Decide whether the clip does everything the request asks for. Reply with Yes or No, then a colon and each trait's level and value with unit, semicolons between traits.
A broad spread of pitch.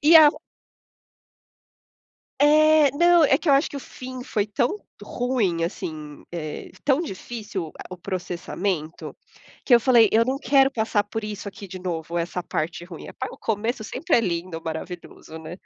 Yes: wide, 7.4 semitones